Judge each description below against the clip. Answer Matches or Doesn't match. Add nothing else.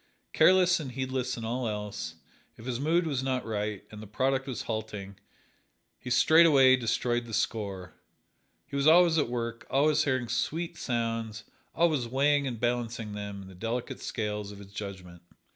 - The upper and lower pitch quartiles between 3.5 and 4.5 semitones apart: Matches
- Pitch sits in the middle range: Doesn't match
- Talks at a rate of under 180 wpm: Matches